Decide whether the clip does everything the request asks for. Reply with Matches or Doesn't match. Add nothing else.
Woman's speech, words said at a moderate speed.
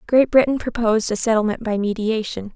Matches